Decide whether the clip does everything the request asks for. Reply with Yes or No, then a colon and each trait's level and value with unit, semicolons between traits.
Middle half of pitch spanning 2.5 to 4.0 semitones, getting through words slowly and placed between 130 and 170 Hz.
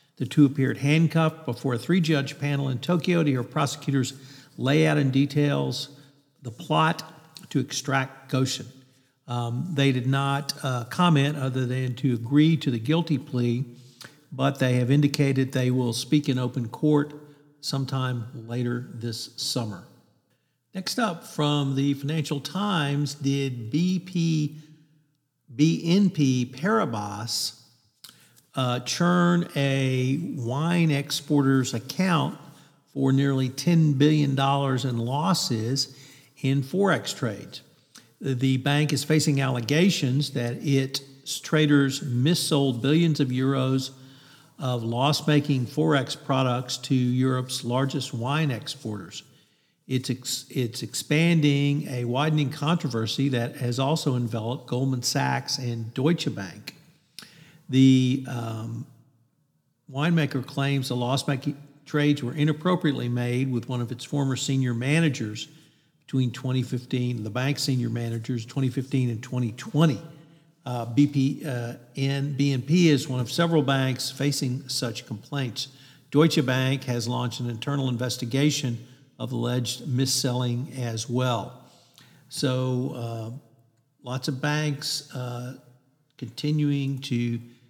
Yes: average, 2.8 semitones; slow, 120 wpm; low, 135 Hz